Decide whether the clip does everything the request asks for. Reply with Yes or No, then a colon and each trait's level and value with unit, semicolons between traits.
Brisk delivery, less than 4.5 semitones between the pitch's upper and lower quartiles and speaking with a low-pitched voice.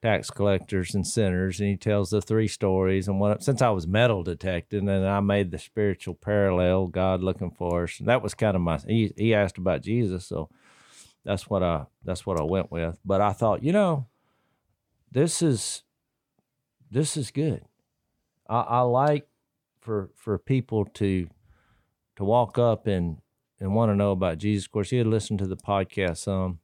No: average, 190 wpm; average, 3.5 semitones; low, 100 Hz